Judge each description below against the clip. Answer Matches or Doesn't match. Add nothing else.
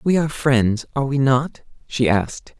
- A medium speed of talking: Matches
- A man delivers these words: Matches